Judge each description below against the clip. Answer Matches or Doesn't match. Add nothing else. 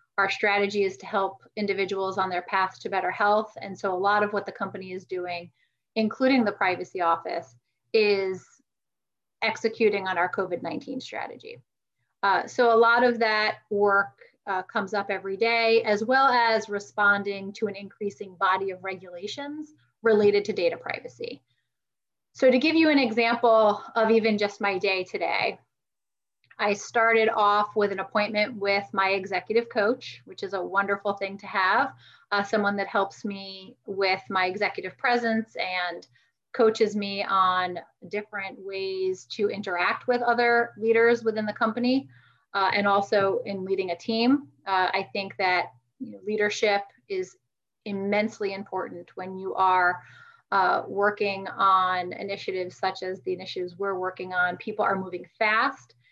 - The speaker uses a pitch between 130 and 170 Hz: Doesn't match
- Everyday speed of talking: Matches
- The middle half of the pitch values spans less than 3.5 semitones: Matches